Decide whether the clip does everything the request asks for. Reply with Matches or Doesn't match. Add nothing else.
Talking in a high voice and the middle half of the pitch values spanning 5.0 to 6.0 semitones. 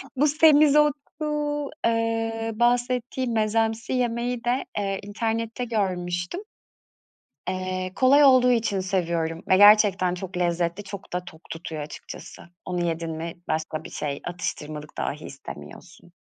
Matches